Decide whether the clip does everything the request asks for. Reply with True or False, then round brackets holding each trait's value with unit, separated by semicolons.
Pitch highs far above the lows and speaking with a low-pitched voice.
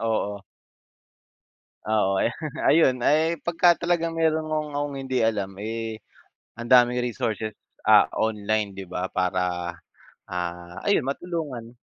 True (6.5 semitones; 115 Hz)